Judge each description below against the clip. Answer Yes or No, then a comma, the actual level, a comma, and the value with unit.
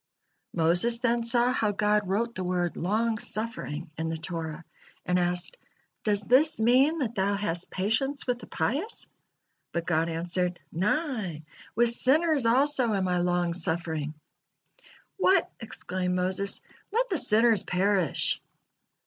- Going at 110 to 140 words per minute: Yes, slow, 135 wpm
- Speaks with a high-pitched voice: Yes, high, 205 Hz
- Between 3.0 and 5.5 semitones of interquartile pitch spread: Yes, average, 5.2 semitones